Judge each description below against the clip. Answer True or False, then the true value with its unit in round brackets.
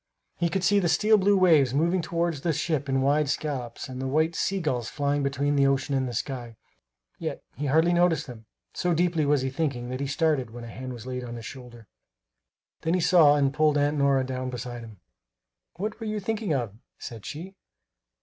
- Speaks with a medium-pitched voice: True (145 Hz)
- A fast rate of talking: True (210 wpm)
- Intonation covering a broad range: False (4.6 semitones)